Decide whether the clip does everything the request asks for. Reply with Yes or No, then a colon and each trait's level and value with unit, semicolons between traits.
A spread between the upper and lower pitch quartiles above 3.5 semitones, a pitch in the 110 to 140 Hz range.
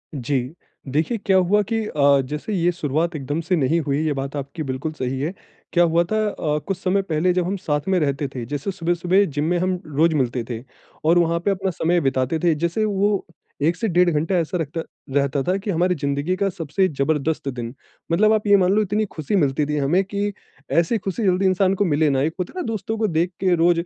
No: average, 4.4 semitones; medium, 170 Hz